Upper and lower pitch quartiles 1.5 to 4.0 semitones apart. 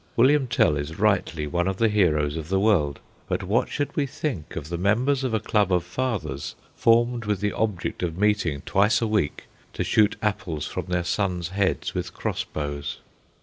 No: average, 5.2 semitones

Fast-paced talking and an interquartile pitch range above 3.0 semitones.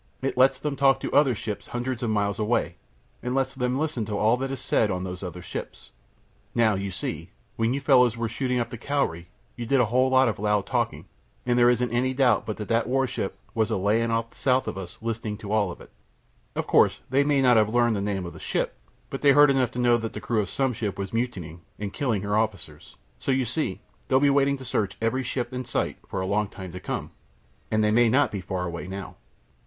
Yes: fast, 245 wpm; average, 4.1 semitones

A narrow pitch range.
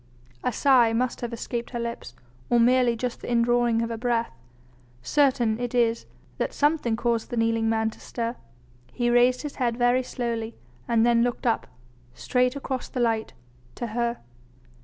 Yes: narrow, 1.3 semitones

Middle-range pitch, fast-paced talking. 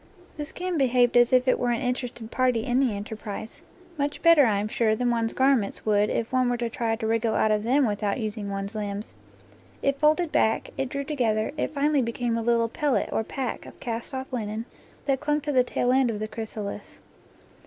No: high, 240 Hz; fast, 215 wpm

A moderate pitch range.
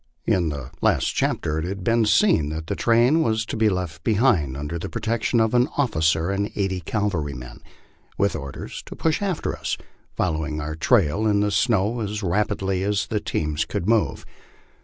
No: wide, 5.9 semitones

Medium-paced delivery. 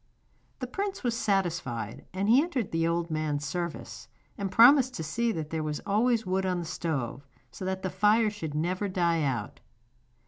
Yes: average, 180 wpm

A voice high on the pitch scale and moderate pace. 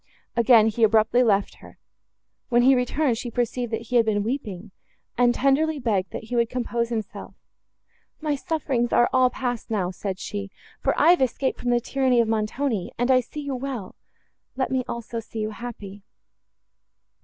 Yes: high, 240 Hz; average, 175 wpm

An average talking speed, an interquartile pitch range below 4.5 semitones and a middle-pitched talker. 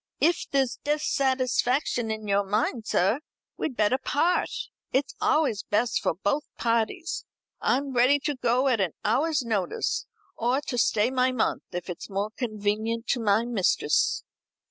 No: average, 145 wpm; average, 4.1 semitones; high, 240 Hz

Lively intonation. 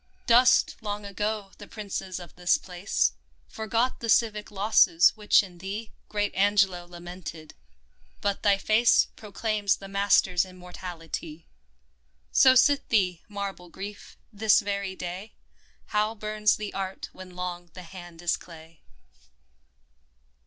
No: average, 3.0 semitones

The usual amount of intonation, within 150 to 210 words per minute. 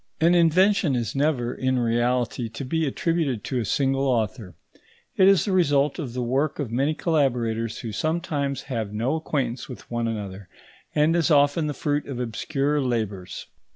Yes: average, 4.4 semitones; average, 170 wpm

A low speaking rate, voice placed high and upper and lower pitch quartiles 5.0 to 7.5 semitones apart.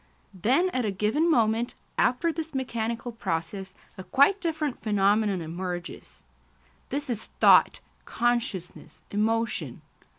Yes: slow, 110 wpm; high, 225 Hz; average, 5.3 semitones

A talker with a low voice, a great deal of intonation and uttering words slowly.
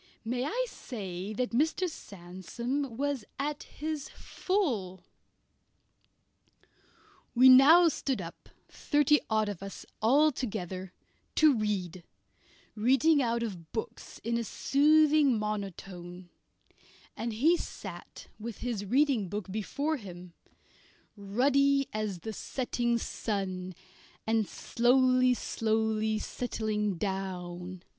No: high, 225 Hz; wide, 5.9 semitones; slow, 105 wpm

